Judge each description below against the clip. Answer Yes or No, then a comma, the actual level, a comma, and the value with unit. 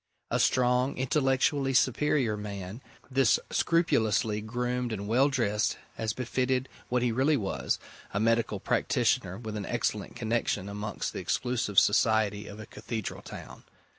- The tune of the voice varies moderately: Yes, average, 3.3 semitones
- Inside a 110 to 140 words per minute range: Yes, slow, 135 wpm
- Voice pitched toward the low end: Yes, low, 115 Hz